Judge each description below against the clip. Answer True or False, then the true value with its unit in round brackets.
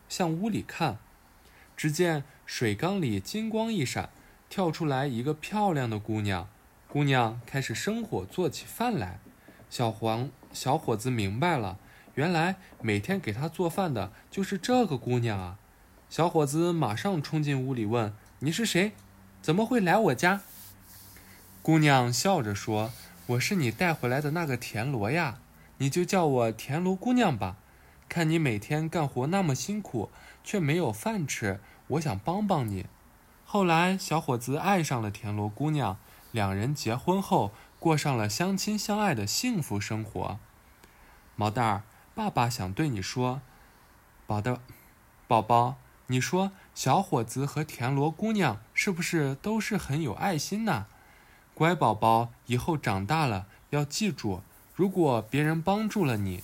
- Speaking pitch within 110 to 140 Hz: True (135 Hz)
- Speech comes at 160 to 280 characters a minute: True (215 characters per minute)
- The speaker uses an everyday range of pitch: False (7.9 semitones)